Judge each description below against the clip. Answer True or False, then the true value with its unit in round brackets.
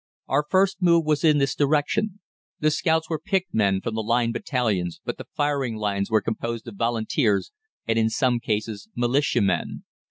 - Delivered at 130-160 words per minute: False (170 wpm)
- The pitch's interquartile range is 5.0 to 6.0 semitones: True (5.6 semitones)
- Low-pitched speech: True (120 Hz)